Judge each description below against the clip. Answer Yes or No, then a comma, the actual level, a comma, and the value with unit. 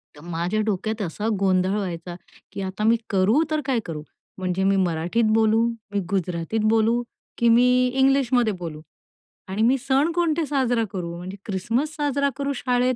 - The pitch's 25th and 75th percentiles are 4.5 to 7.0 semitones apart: Yes, average, 5.2 semitones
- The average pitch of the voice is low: No, high, 220 Hz